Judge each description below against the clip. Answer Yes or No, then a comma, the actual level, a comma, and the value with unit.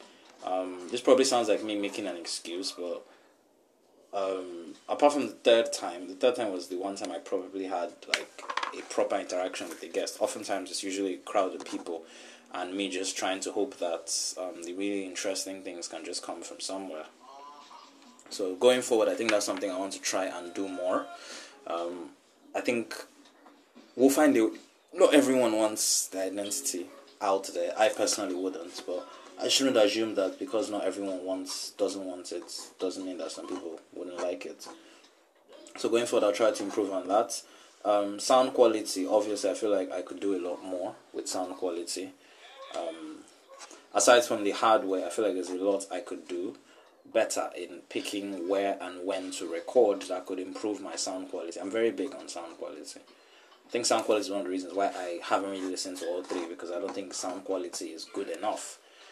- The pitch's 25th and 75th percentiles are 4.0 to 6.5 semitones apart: No, average, 3.1 semitones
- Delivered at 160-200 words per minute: Yes, average, 195 wpm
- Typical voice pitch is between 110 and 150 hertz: No, low, 100 Hz